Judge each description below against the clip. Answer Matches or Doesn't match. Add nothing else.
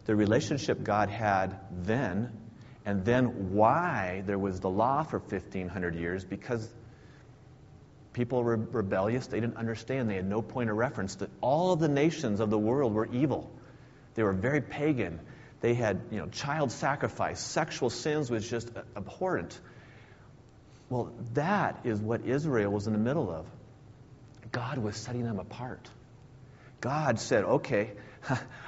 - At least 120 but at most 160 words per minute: Matches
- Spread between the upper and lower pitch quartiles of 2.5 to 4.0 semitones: Matches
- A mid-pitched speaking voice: Doesn't match